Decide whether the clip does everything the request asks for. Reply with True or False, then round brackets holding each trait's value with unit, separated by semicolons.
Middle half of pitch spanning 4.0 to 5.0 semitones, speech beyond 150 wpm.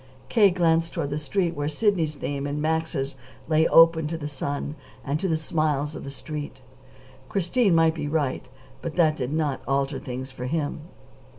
False (2.6 semitones; 180 wpm)